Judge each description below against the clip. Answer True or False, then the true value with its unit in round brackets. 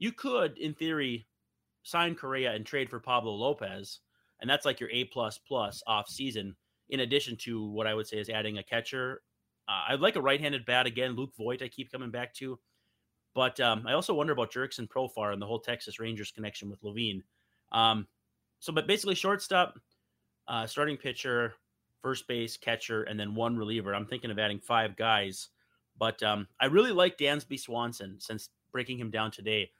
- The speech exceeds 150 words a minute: True (190 wpm)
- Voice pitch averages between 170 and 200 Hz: False (115 Hz)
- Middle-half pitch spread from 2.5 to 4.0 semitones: True (3.5 semitones)